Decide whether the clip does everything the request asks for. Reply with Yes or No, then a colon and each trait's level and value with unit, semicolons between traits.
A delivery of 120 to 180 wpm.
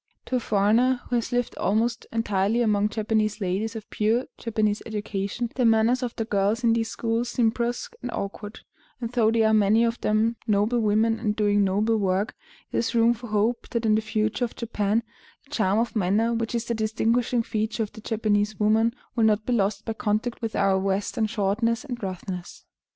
No: average, 200 wpm